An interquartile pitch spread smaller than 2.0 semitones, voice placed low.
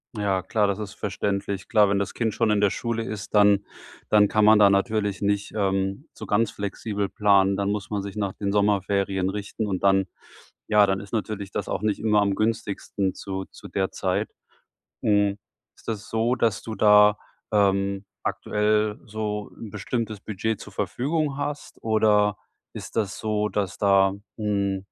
Yes: narrow, 1.5 semitones; low, 105 Hz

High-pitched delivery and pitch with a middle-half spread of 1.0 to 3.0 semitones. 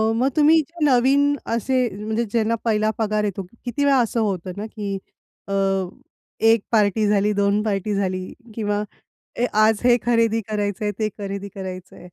Yes: high, 215 Hz; average, 2.7 semitones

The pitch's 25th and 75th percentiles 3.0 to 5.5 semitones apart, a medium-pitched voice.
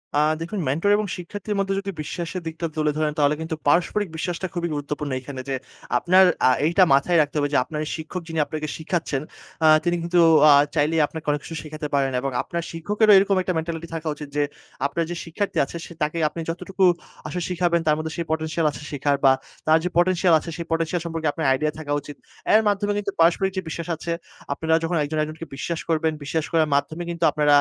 No: narrow, 2.5 semitones; medium, 165 Hz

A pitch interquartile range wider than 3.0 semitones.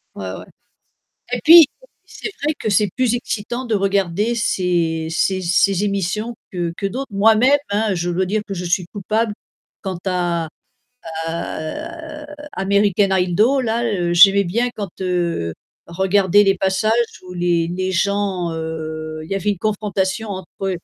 Yes: average, 3.5 semitones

